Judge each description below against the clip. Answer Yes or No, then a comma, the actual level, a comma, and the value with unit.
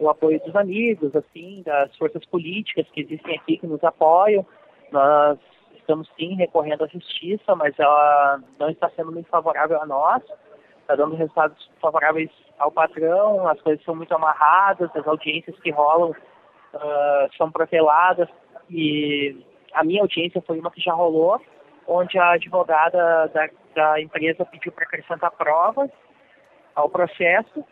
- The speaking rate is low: No, average, 145 wpm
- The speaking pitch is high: No, medium, 165 Hz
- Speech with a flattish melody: Yes, narrow, 2.3 semitones